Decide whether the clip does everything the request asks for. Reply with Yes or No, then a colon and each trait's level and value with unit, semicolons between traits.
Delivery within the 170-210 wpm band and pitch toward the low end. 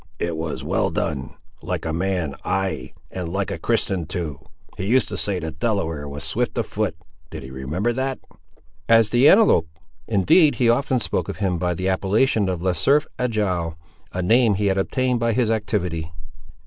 Yes: average, 180 wpm; very low, 95 Hz